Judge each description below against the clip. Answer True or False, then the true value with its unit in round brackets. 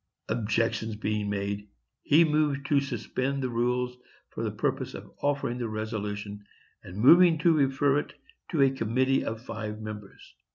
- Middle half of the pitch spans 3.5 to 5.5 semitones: True (4.5 semitones)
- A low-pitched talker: True (125 Hz)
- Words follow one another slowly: False (155 wpm)